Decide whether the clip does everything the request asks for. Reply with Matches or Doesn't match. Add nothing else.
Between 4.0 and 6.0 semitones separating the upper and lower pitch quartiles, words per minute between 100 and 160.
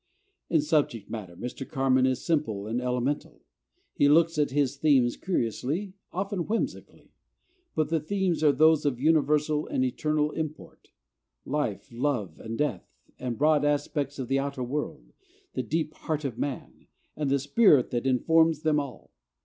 Doesn't match